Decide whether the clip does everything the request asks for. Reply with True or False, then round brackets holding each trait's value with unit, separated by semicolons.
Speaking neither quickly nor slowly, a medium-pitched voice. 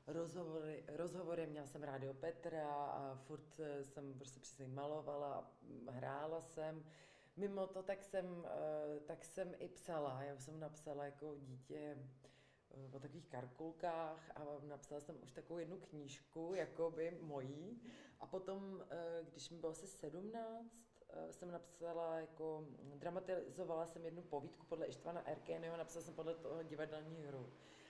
True (140 wpm; 160 Hz)